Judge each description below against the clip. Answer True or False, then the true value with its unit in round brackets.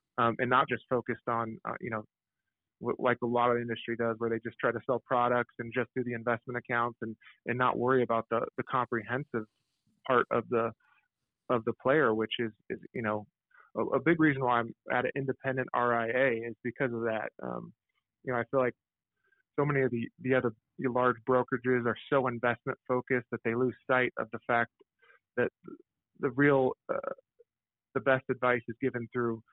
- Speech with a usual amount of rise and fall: False (1.8 semitones)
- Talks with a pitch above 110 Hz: True (120 Hz)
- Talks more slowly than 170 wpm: False (200 wpm)